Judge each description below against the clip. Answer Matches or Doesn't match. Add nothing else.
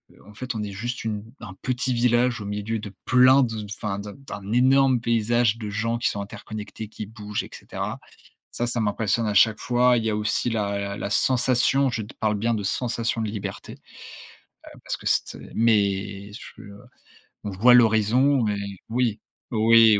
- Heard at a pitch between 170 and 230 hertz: Doesn't match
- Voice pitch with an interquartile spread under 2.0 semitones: Doesn't match